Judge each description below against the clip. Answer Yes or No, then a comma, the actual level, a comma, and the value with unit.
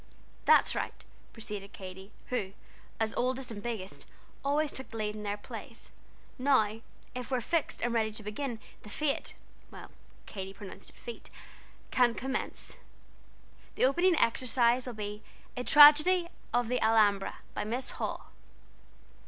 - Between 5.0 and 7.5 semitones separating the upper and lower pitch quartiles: No, average, 3.9 semitones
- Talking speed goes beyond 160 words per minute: No, average, 140 wpm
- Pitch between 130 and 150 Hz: No, high, 235 Hz